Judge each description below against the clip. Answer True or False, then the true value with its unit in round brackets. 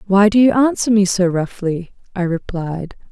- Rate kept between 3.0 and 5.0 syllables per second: True (4.6 syllables/s)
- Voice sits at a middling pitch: False (195 Hz)